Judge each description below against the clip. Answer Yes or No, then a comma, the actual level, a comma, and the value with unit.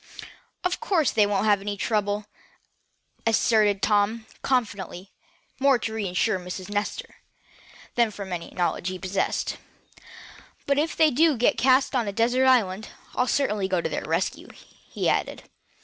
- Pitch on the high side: Yes, high, 215 Hz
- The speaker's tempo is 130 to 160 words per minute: Yes, average, 150 wpm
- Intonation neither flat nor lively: Yes, average, 4.3 semitones